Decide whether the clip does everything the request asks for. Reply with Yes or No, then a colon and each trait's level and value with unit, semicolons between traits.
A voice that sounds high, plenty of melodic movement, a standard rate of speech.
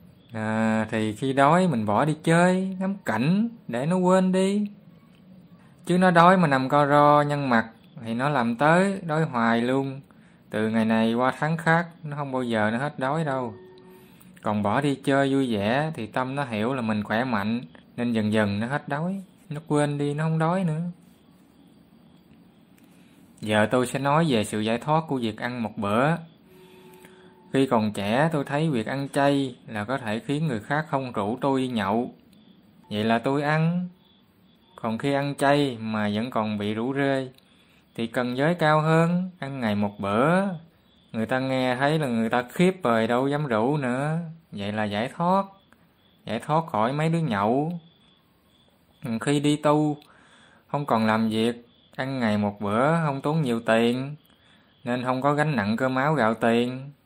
No: medium, 140 Hz; wide, 6.1 semitones; average, 180 wpm